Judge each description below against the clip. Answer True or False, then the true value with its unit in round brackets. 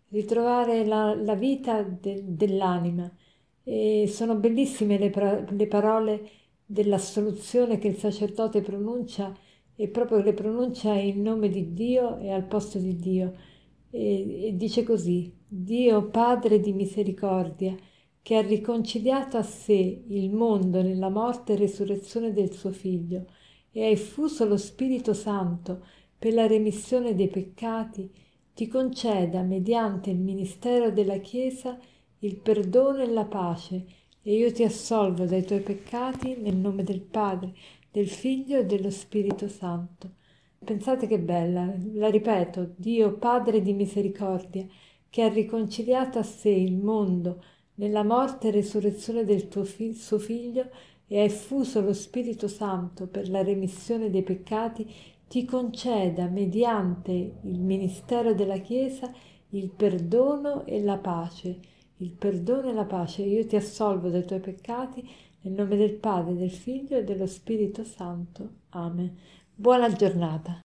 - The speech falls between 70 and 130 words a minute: False (140 wpm)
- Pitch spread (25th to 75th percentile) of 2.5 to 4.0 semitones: True (2.9 semitones)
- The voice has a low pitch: False (205 Hz)